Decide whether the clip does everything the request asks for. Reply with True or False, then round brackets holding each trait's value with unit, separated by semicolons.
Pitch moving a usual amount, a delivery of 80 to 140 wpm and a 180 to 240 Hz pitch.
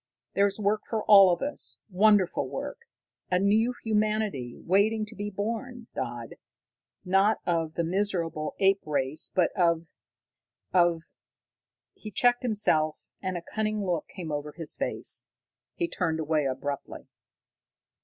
True (4.7 semitones; 135 wpm; 190 Hz)